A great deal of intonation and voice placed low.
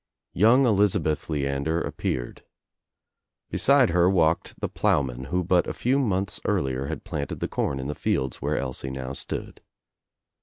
Yes: wide, 6.2 semitones; very low, 80 Hz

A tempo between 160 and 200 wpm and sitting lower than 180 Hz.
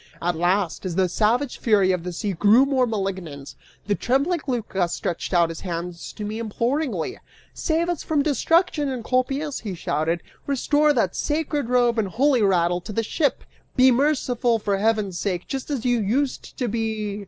No: average, 175 wpm; high, 225 Hz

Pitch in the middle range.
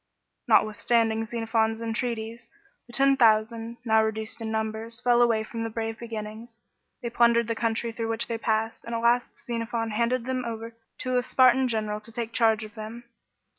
No: high, 230 Hz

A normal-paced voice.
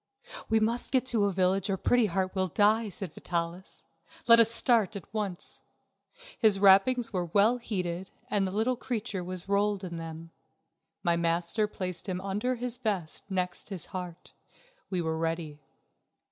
Yes: average, 160 wpm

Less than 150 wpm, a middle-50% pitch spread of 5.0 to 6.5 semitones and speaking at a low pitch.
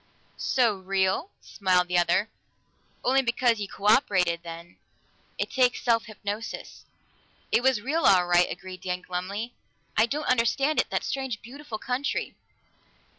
No: average, 140 wpm; wide, 5.4 semitones; high, 215 Hz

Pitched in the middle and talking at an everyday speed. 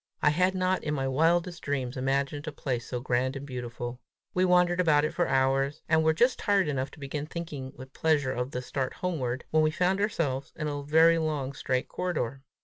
No: medium, 145 Hz; fast, 210 wpm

